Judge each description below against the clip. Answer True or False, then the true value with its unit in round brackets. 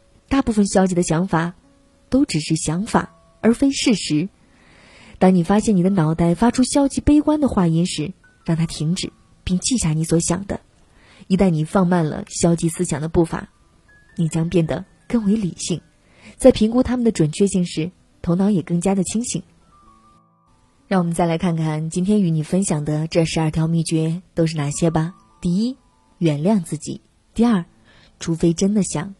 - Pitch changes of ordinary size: True (3.5 semitones)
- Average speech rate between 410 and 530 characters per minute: False (255 characters per minute)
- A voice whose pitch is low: False (180 Hz)